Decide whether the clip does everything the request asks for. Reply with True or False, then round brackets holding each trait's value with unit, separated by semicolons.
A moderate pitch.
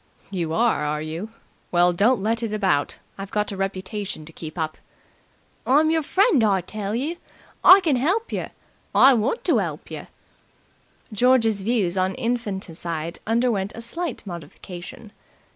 False (210 Hz)